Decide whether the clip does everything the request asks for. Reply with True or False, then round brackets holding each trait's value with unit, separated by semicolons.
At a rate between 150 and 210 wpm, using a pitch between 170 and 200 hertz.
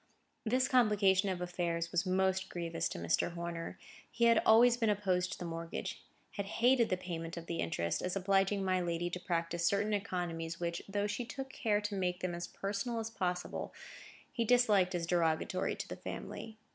True (185 wpm; 185 Hz)